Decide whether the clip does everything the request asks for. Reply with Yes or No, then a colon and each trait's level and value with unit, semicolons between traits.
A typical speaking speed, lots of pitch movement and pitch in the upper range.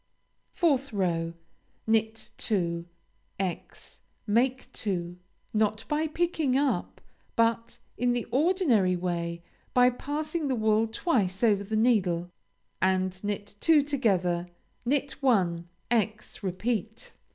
No: slow, 110 wpm; wide, 5.8 semitones; high, 220 Hz